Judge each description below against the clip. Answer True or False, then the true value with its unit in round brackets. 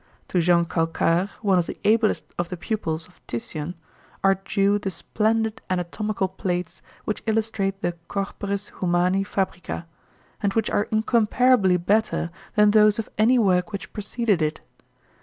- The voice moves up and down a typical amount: True (3.3 semitones)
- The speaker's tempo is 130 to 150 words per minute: True (145 wpm)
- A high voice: True (195 Hz)